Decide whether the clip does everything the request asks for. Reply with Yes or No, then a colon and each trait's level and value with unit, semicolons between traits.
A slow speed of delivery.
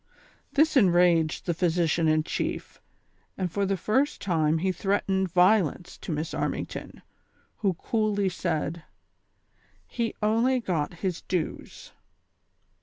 Yes: slow, 115 wpm